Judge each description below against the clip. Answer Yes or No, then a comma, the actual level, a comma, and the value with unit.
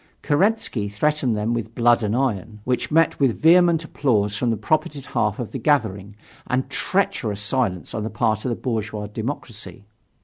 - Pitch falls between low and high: No, low, 115 Hz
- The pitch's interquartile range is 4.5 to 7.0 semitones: Yes, wide, 5.4 semitones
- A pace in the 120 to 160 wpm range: No, average, 170 wpm